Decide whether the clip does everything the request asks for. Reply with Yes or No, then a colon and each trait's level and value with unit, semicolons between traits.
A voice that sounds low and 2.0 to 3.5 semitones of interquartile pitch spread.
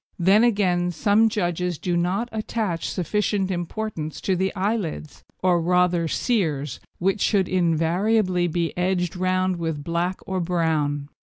No: medium, 180 Hz; narrow, 2.5 semitones